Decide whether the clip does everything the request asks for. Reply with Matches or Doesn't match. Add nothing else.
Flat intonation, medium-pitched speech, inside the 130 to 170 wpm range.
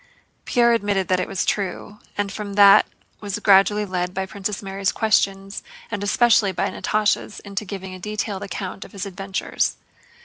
Doesn't match